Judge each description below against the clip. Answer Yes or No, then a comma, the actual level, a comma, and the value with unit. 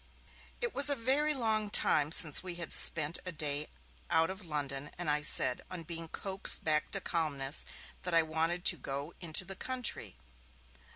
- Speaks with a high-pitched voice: No, medium, 165 Hz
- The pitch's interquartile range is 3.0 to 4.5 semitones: Yes, average, 4.2 semitones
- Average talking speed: Yes, average, 175 wpm